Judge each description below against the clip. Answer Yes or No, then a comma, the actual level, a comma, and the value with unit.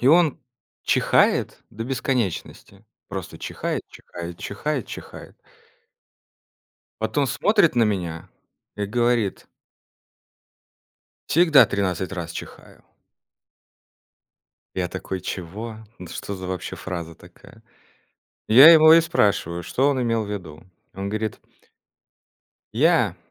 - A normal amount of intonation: No, wide, 6.1 semitones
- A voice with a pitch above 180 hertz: No, low, 105 Hz